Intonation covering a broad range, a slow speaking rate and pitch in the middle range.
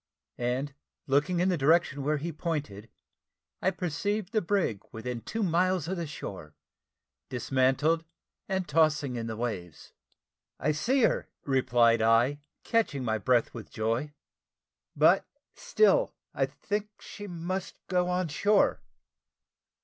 Yes: wide, 7.0 semitones; slow, 130 wpm; medium, 150 Hz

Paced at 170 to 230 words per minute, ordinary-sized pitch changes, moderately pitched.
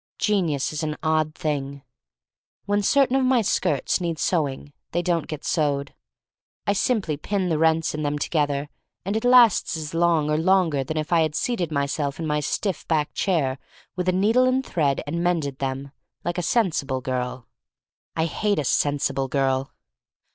Yes: average, 180 wpm; average, 4.4 semitones; medium, 155 Hz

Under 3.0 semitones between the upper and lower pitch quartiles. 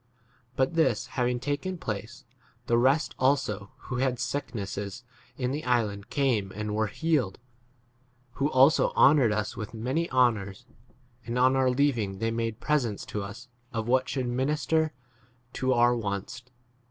No: average, 3.8 semitones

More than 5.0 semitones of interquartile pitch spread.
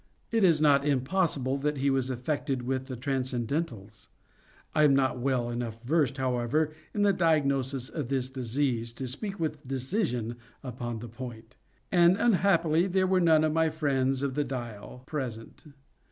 No: average, 3.9 semitones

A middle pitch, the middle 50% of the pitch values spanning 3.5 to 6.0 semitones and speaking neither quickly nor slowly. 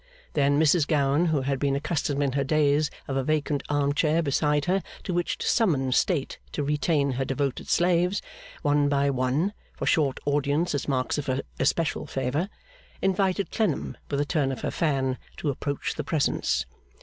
No: medium, 145 Hz; narrow, 2.5 semitones; average, 180 wpm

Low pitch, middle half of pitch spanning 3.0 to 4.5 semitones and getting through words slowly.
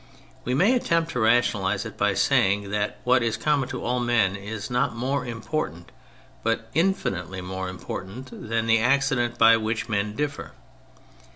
No: low, 115 Hz; average, 3.9 semitones; average, 165 wpm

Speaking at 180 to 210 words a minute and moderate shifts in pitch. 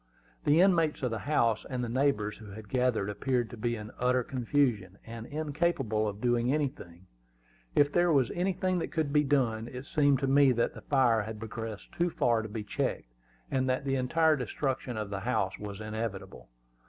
Yes: average, 190 wpm; average, 4.6 semitones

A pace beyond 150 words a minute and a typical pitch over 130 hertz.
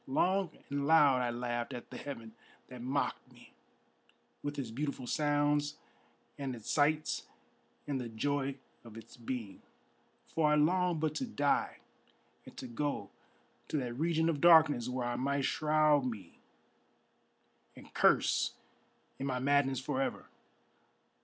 No: average, 140 wpm; medium, 140 Hz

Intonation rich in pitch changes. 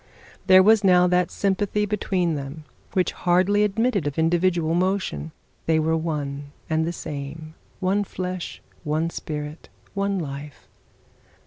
No: average, 3.6 semitones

